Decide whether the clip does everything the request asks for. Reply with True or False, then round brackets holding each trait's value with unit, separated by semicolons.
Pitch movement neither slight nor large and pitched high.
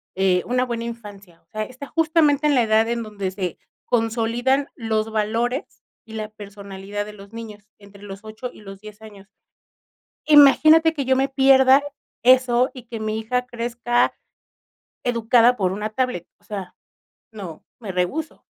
True (3.6 semitones; 225 Hz)